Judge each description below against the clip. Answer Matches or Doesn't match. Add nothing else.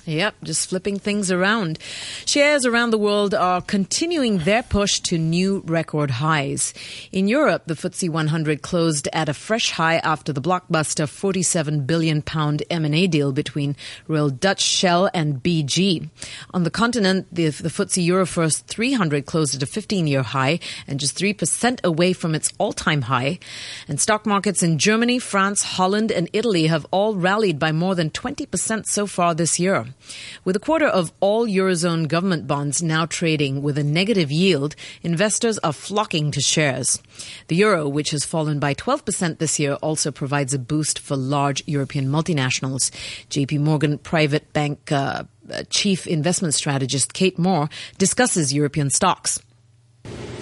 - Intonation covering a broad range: Doesn't match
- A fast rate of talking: Doesn't match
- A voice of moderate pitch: Matches